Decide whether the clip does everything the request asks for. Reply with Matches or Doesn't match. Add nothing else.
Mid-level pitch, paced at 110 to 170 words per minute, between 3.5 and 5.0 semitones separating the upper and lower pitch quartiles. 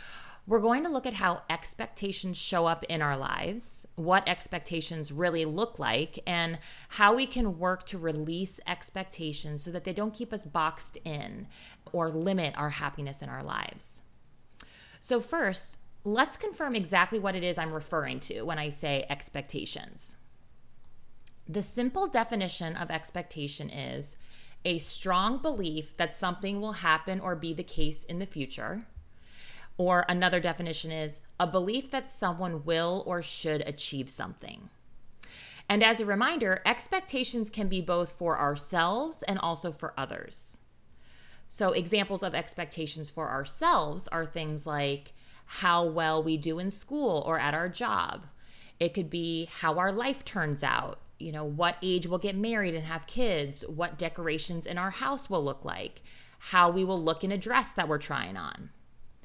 Matches